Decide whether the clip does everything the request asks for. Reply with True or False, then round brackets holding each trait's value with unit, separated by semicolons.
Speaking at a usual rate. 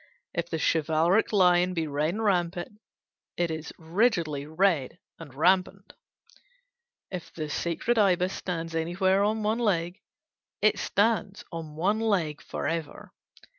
False (130 wpm)